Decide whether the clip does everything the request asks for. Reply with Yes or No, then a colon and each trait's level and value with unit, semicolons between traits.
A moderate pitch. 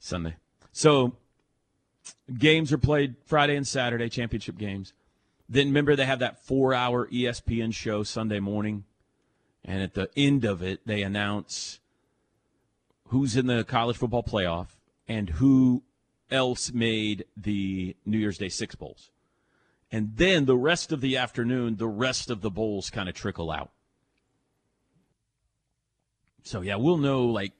No: low, 120 Hz